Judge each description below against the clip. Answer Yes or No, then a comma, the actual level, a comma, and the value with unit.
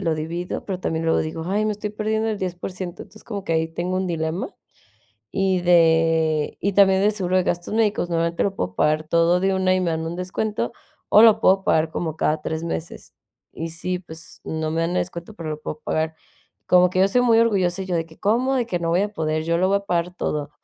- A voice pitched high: No, medium, 175 Hz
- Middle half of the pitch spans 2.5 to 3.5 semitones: Yes, average, 3.1 semitones